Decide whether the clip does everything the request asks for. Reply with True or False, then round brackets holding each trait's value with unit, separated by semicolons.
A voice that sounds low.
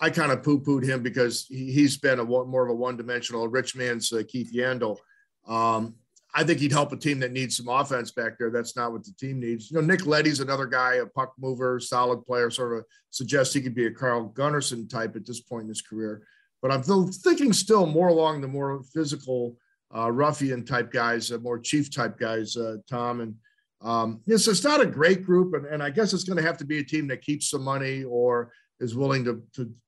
True (130 Hz)